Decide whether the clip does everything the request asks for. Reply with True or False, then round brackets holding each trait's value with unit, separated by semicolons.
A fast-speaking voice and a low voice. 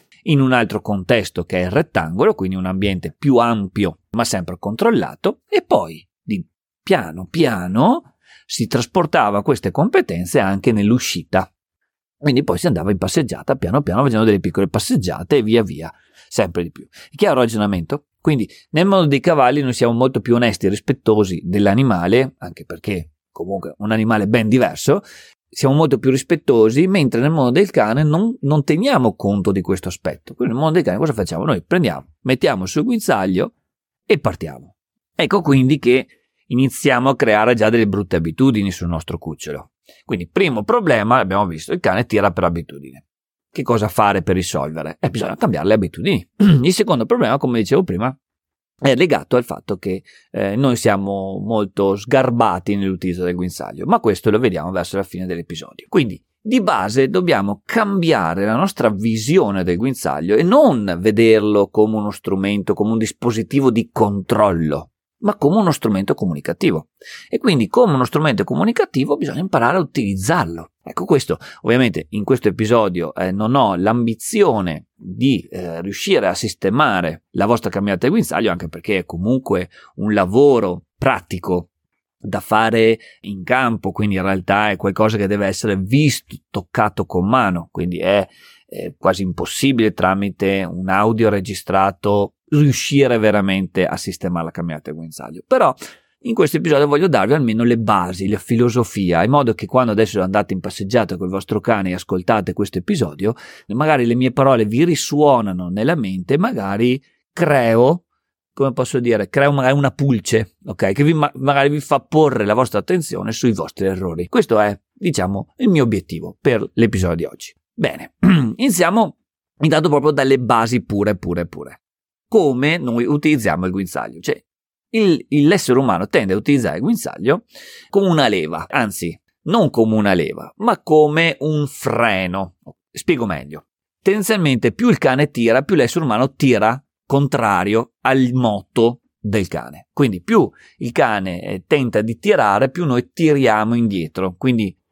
False (160 wpm; 110 Hz)